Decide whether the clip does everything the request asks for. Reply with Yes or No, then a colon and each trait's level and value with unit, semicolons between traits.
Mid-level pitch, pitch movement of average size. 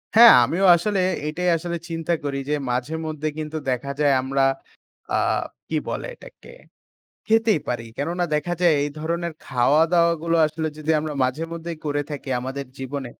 Yes: medium, 155 Hz; average, 3.2 semitones